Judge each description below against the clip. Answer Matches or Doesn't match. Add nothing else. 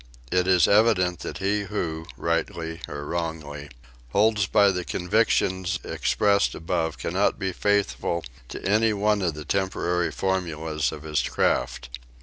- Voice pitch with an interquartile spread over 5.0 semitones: Doesn't match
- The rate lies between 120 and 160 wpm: Matches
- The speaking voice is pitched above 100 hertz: Doesn't match